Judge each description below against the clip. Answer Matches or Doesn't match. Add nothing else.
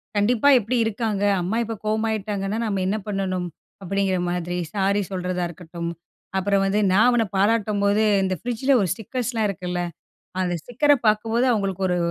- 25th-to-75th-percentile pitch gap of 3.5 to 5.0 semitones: Doesn't match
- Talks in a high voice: Matches